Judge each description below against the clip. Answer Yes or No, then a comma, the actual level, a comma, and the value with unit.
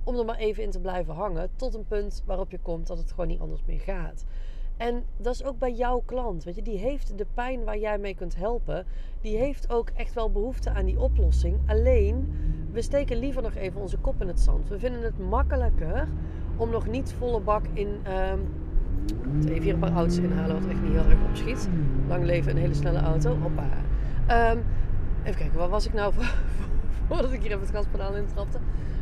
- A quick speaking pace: Yes, fast, 215 wpm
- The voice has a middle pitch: Yes, medium, 175 Hz